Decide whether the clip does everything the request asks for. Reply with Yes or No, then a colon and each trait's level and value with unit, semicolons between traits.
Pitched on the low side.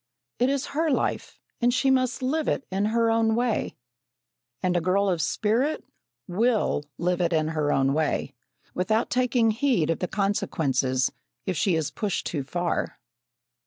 No: high, 200 Hz